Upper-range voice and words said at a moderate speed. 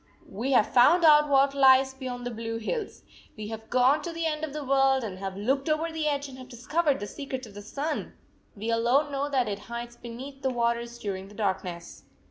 No: very high, 255 Hz; fast, 225 wpm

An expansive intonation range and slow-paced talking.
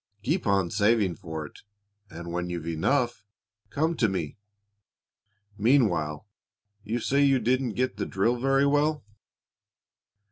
Yes: wide, 7.6 semitones; slow, 130 wpm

